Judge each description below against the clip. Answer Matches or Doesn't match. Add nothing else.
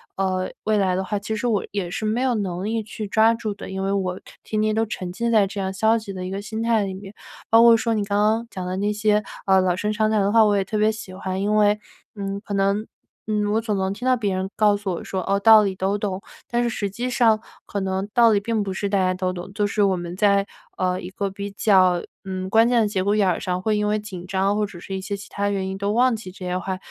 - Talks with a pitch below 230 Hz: Matches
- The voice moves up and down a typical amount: Doesn't match